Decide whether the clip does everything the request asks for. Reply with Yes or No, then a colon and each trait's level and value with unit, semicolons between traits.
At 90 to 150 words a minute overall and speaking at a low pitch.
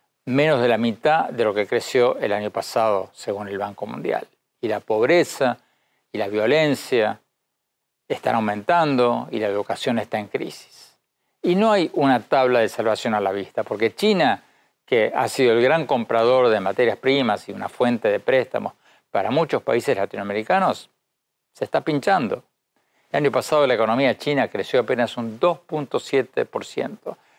No: average, 160 wpm; low, 130 Hz